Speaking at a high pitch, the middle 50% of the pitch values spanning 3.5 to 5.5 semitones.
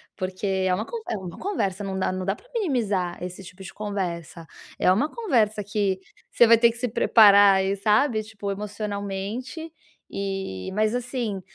No: high, 205 Hz; average, 3.1 semitones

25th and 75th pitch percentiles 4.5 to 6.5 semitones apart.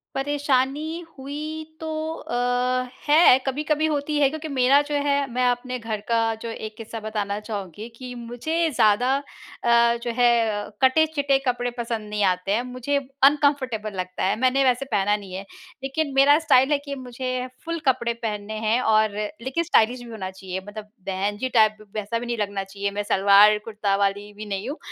Yes: average, 4.8 semitones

